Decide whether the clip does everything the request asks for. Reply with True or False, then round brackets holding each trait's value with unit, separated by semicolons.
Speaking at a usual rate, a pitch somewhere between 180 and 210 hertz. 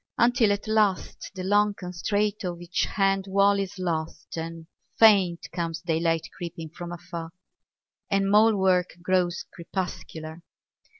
False (130 wpm; 185 Hz)